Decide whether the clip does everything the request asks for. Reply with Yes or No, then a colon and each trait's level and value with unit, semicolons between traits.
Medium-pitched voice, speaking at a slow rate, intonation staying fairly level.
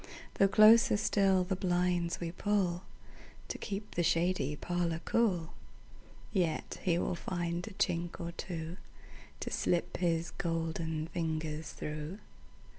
Yes: medium, 175 Hz; slow, 115 wpm; narrow, 2.3 semitones